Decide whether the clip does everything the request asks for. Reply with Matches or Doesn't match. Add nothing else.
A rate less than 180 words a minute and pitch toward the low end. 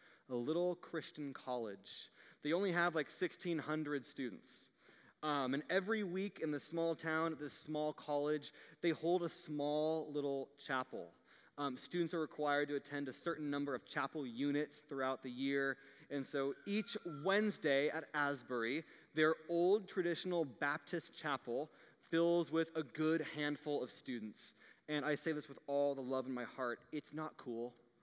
Doesn't match